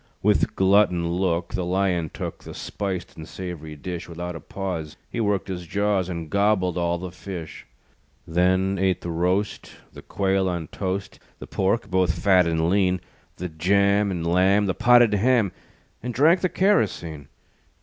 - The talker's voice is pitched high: No, very low, 95 Hz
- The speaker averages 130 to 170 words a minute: Yes, average, 160 wpm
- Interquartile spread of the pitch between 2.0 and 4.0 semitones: Yes, narrow, 2.5 semitones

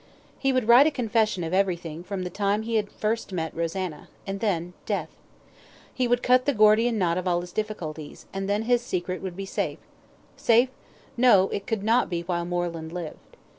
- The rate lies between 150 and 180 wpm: No, average, 195 wpm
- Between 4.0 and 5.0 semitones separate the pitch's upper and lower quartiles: Yes, average, 4.3 semitones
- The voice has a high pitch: Yes, high, 195 Hz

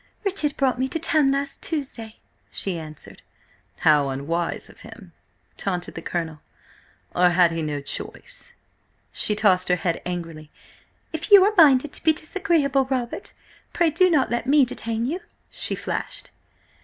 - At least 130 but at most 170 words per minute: Yes, average, 155 wpm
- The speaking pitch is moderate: No, high, 240 Hz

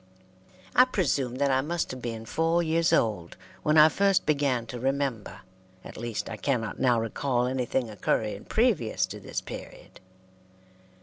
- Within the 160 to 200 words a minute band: No, average, 150 wpm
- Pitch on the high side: No, low, 130 Hz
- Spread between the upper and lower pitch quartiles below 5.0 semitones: No, average, 5.3 semitones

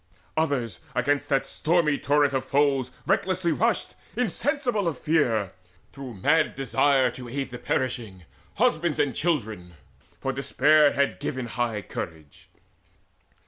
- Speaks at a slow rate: Yes, slow, 125 wpm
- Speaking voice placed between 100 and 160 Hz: Yes, medium, 140 Hz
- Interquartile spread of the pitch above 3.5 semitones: Yes, average, 4.2 semitones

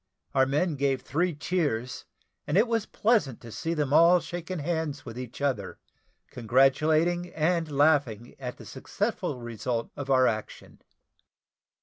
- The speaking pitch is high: No, medium, 145 Hz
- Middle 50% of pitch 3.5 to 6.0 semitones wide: Yes, average, 4.8 semitones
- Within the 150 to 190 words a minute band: No, average, 140 wpm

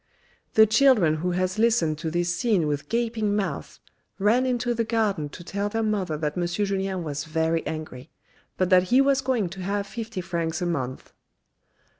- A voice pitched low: No, high, 190 Hz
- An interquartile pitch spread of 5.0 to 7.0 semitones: Yes, average, 5.3 semitones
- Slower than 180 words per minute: No, average, 185 wpm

